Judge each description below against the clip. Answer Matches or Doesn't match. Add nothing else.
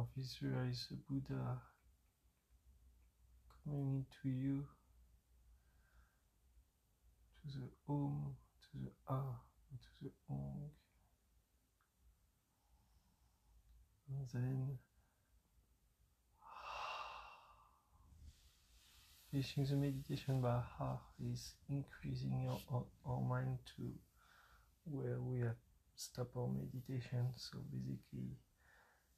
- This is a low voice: Matches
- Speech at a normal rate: Doesn't match